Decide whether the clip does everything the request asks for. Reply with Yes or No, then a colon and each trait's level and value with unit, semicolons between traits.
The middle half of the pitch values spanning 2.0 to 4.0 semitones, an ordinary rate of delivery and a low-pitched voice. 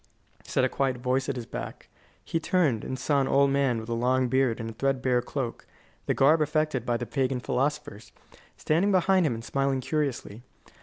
Yes: average, 2.9 semitones; average, 195 wpm; low, 130 Hz